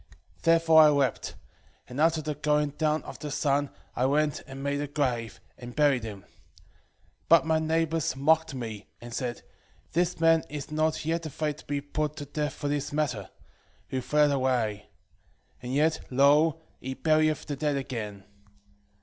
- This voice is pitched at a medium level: Yes, medium, 145 Hz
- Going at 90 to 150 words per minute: No, average, 170 wpm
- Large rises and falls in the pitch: No, average, 2.9 semitones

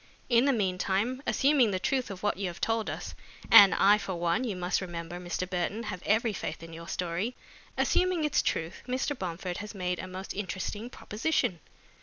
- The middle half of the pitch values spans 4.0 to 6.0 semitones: Yes, average, 4.4 semitones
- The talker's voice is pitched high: Yes, high, 195 Hz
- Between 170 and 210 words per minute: Yes, average, 190 wpm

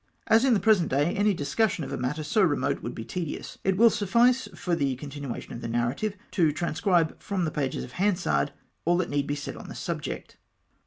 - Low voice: No, medium, 165 Hz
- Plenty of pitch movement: Yes, wide, 6.3 semitones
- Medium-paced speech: No, fast, 215 wpm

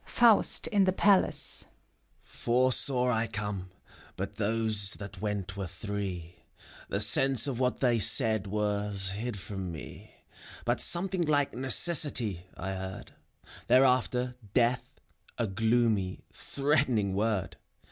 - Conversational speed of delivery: No, slow, 125 wpm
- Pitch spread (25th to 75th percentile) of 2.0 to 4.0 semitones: No, average, 4.5 semitones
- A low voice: Yes, low, 110 Hz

